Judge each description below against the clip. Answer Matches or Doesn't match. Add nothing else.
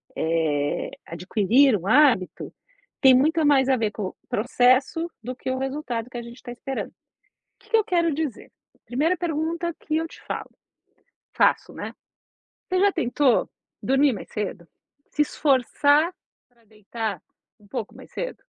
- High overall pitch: Matches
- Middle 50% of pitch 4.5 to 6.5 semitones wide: Matches